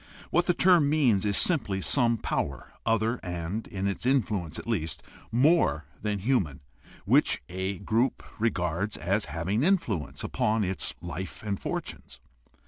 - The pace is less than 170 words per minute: Yes, average, 140 wpm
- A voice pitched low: Yes, low, 105 Hz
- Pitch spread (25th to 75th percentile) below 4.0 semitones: No, average, 4.7 semitones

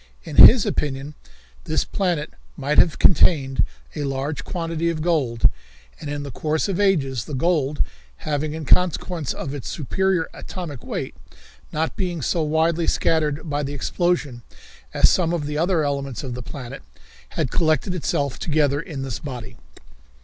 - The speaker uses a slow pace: No, average, 155 wpm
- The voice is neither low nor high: Yes, medium, 150 Hz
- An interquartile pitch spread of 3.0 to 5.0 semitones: Yes, average, 3.4 semitones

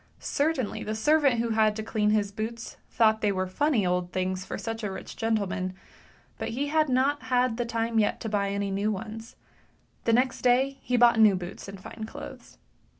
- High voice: Yes, high, 220 Hz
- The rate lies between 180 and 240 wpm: Yes, average, 195 wpm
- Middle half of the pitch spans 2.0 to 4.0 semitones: Yes, average, 3.5 semitones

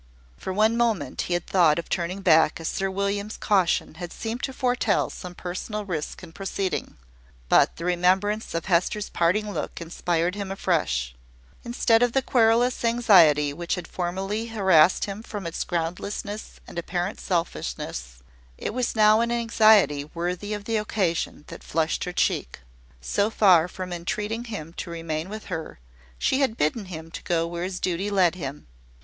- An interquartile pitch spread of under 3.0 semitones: No, average, 4.1 semitones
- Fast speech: No, average, 165 wpm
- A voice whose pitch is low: No, medium, 185 Hz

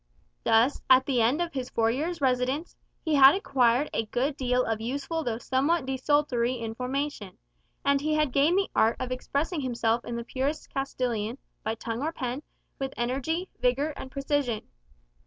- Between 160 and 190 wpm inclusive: Yes, average, 170 wpm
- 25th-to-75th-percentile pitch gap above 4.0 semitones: No, average, 3.3 semitones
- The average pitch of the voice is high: Yes, very high, 260 Hz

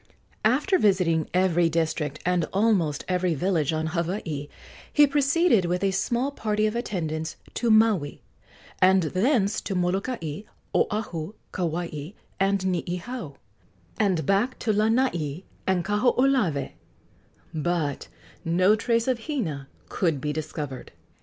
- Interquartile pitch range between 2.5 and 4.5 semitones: No, average, 5.2 semitones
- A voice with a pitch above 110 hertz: Yes, medium, 185 Hz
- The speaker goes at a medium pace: No, slow, 120 wpm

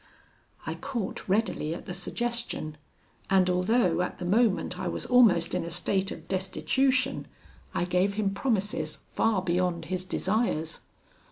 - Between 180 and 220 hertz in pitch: Yes, high, 190 Hz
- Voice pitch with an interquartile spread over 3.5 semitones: Yes, average, 4.0 semitones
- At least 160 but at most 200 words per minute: No, average, 145 wpm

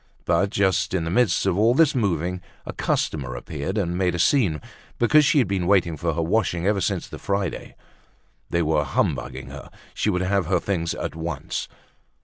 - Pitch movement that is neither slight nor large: Yes, average, 3.5 semitones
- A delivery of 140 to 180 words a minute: No, average, 190 wpm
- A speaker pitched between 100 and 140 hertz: No, very low, 90 Hz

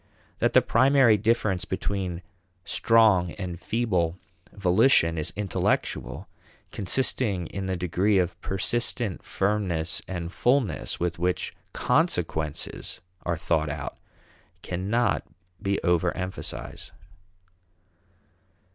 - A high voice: No, very low, 95 Hz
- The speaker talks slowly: Yes, slow, 95 wpm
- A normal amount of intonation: Yes, average, 3.5 semitones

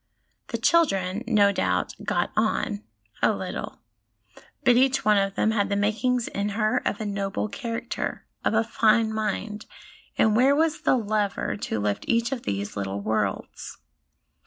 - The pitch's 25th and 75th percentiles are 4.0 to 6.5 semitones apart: No, average, 3.1 semitones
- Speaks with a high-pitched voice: Yes, high, 215 Hz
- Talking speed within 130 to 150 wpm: No, average, 160 wpm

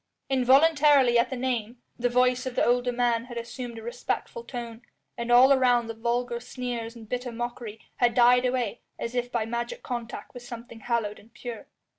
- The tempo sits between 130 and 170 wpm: No, average, 185 wpm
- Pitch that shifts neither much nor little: No, narrow, 1.1 semitones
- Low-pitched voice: No, high, 245 Hz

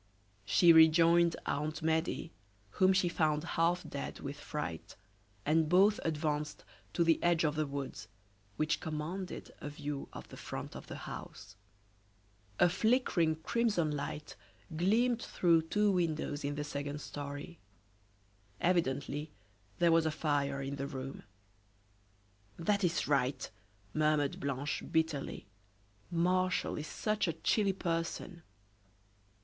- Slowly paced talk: Yes, slow, 125 wpm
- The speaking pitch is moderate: Yes, medium, 160 Hz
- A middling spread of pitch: Yes, average, 3.0 semitones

